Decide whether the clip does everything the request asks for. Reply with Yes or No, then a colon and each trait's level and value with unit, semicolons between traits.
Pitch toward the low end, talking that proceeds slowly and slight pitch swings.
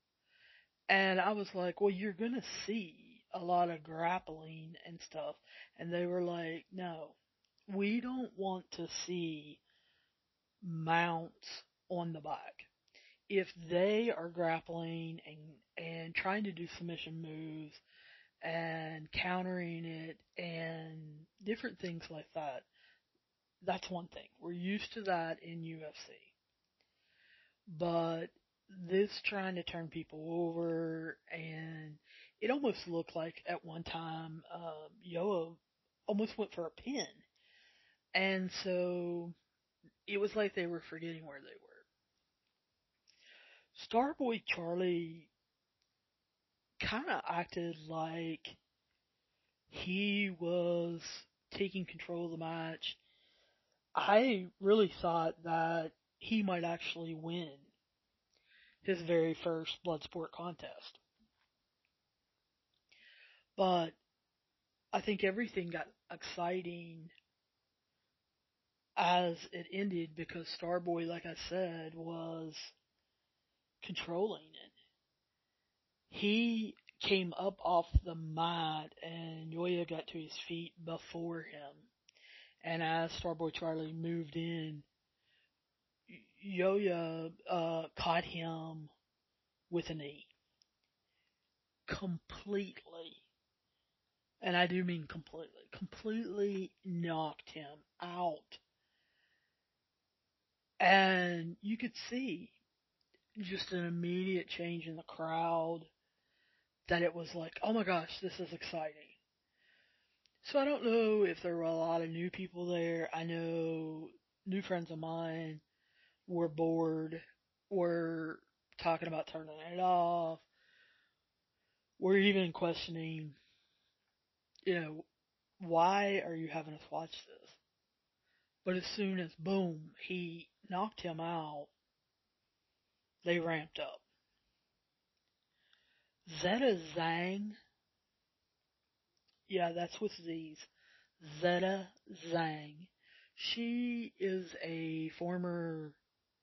No: medium, 170 Hz; slow, 105 wpm; narrow, 2.3 semitones